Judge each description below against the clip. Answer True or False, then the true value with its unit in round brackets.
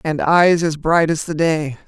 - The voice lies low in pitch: False (160 Hz)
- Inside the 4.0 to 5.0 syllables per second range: True (4.1 syllables/s)